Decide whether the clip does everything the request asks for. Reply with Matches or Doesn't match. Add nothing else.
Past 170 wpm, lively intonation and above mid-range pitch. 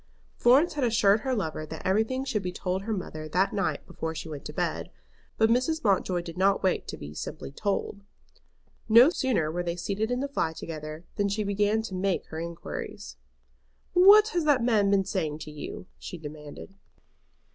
Matches